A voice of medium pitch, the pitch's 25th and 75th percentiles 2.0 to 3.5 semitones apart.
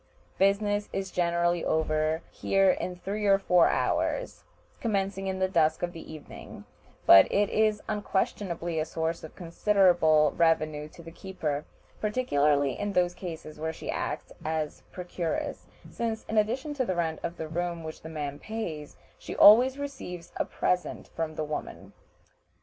No: medium, 175 Hz; average, 4.1 semitones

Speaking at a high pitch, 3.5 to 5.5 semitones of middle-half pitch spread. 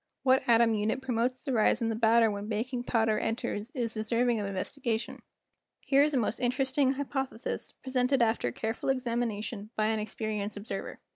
No: high, 230 Hz; average, 2.9 semitones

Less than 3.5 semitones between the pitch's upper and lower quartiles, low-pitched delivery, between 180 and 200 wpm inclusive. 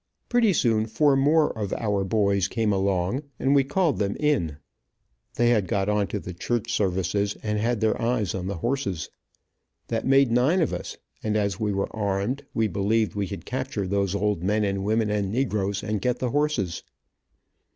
No: average, 3.9 semitones; low, 105 Hz; average, 185 wpm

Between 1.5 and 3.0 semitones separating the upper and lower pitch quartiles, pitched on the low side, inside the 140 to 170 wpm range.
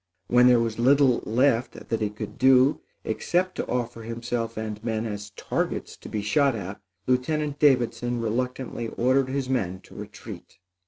Yes: average, 2.7 semitones; low, 120 Hz; average, 160 wpm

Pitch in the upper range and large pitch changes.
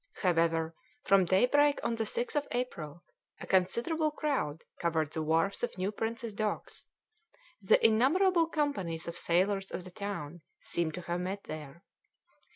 Yes: high, 195 Hz; wide, 6.3 semitones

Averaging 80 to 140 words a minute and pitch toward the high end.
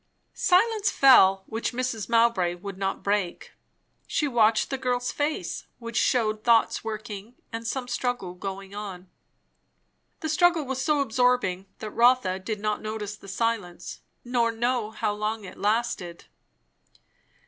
Yes: slow, 135 wpm; high, 225 Hz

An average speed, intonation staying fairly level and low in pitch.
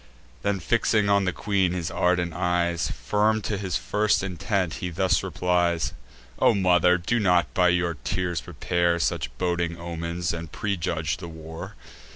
Yes: average, 155 wpm; narrow, 2.0 semitones; very low, 90 Hz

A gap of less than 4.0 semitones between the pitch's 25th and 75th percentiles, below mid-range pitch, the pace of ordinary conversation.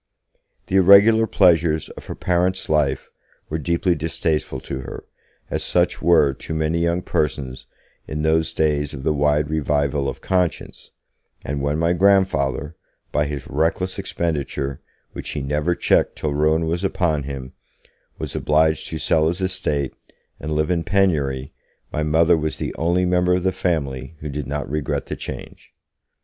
Yes: average, 3.1 semitones; very low, 80 Hz; average, 160 wpm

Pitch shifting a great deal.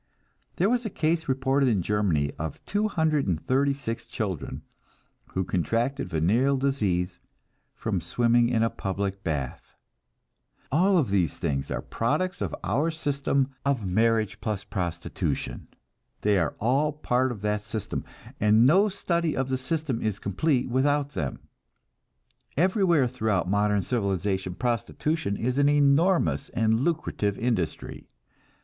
Yes: wide, 6.2 semitones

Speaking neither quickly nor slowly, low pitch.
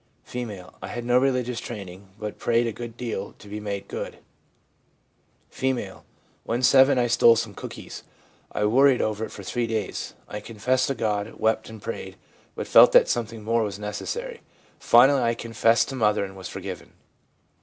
Yes: average, 175 wpm; low, 115 Hz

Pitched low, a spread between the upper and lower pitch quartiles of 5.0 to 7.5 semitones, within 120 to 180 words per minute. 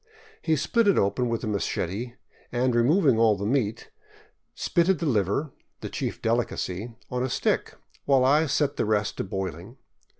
Yes: low, 120 Hz; average, 5.3 semitones; average, 165 wpm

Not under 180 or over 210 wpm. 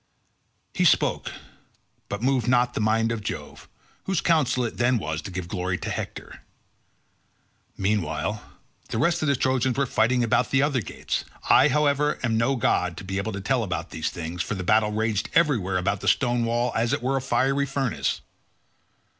Yes: average, 190 wpm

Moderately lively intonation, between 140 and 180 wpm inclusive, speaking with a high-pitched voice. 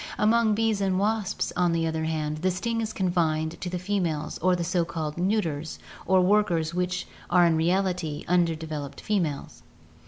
No: average, 3.2 semitones; average, 175 wpm; medium, 180 Hz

